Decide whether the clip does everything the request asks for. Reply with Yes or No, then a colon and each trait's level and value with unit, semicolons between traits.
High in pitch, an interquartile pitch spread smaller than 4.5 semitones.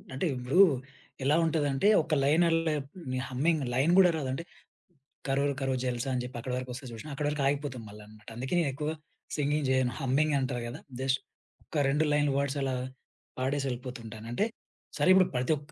No: low, 135 Hz; average, 2.8 semitones